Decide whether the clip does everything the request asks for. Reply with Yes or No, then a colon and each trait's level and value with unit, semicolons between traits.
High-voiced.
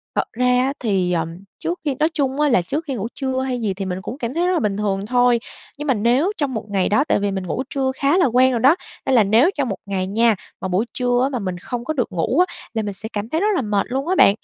Yes: high, 245 Hz